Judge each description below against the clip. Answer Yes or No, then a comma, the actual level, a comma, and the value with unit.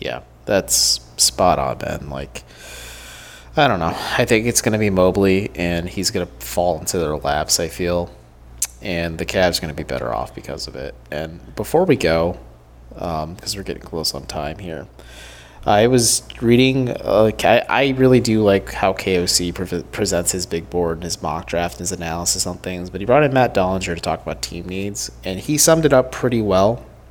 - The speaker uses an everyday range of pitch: Yes, average, 4.6 semitones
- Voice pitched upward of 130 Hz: No, very low, 90 Hz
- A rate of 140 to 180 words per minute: No, average, 200 wpm